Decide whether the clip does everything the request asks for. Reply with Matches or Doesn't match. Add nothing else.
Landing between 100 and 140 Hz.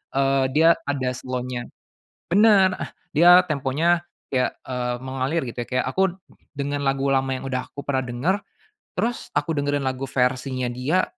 Matches